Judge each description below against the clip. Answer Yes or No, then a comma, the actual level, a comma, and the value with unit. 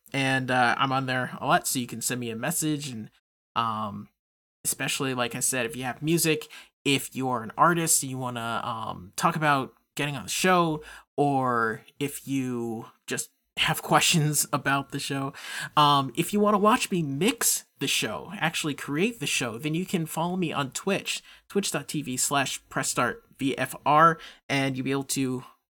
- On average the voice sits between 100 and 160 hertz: Yes, low, 135 Hz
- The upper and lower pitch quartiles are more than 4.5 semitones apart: No, average, 3.8 semitones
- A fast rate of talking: No, average, 180 wpm